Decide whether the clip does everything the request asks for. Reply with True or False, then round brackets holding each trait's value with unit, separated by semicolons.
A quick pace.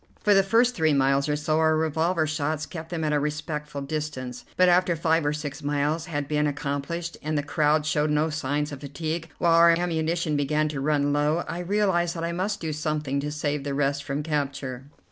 True (210 wpm)